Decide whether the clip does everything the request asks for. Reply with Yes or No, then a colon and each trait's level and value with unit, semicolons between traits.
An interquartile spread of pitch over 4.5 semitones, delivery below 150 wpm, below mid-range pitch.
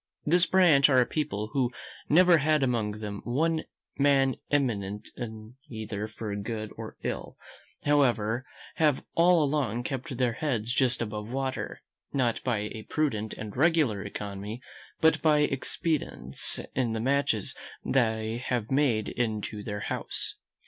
Yes: average, 4.9 semitones; average, 140 wpm; low, 125 Hz